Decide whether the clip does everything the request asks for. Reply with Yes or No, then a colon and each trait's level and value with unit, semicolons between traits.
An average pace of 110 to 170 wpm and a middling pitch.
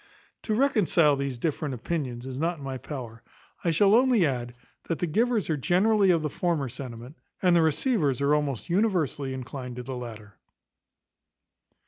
Yes: average, 165 wpm; medium, 150 Hz